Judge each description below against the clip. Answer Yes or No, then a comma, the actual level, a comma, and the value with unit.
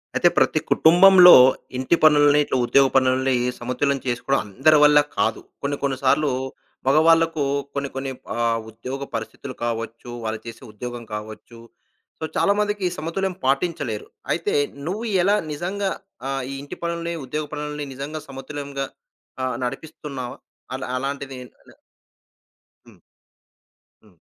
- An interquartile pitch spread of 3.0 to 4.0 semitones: Yes, average, 3.6 semitones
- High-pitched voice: No, medium, 140 Hz